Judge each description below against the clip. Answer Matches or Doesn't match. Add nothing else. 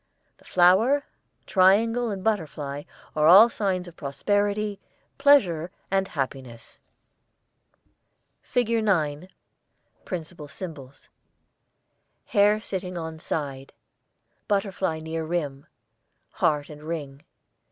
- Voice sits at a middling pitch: Matches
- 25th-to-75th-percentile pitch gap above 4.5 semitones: Matches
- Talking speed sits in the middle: Doesn't match